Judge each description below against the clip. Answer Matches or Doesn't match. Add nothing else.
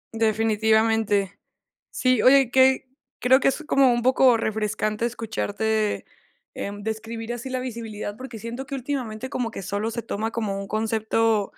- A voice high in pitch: Matches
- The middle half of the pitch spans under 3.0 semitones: Matches